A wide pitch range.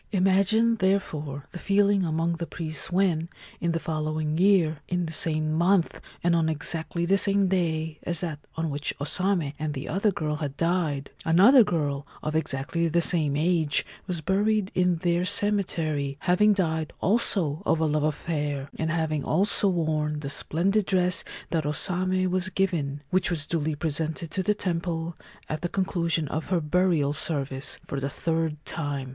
No: average, 3.3 semitones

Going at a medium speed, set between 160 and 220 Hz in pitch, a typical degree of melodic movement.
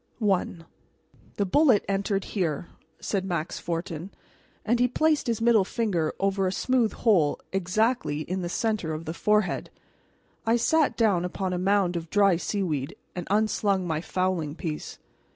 Yes: average, 155 wpm; high, 190 Hz; average, 4.0 semitones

